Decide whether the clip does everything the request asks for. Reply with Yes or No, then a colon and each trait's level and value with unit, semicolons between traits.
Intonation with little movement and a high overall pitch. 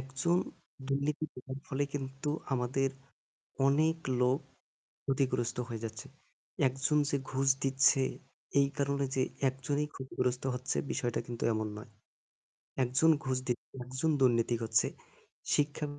No: narrow, 2.0 semitones; low, 135 Hz